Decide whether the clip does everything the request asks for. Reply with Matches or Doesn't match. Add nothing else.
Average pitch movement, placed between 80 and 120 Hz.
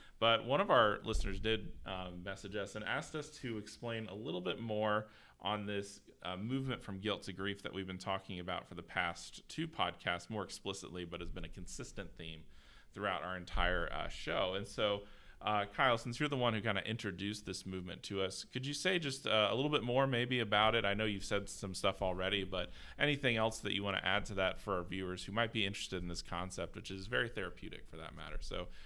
Matches